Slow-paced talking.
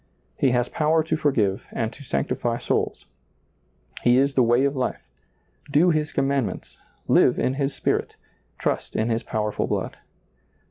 No: average, 150 wpm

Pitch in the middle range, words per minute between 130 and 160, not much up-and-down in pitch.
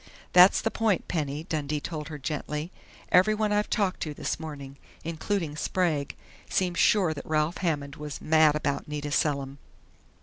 No: medium, 155 Hz; average, 155 wpm; average, 3.5 semitones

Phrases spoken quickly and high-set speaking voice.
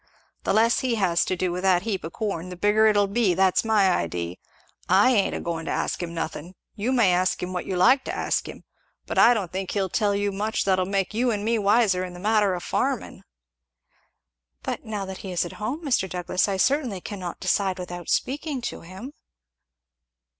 Yes: fast, 210 wpm; high, 195 Hz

